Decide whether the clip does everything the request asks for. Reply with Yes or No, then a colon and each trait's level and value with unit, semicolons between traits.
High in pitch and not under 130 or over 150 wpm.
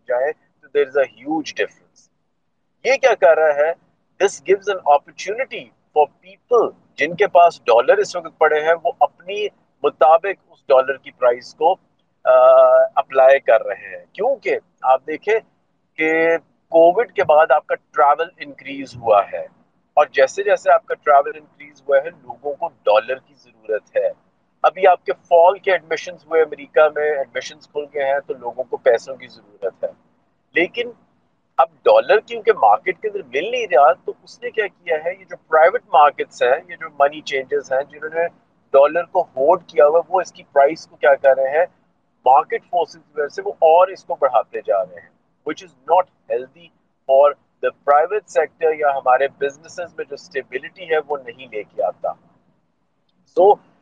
No: medium, 170 Hz; average, 135 wpm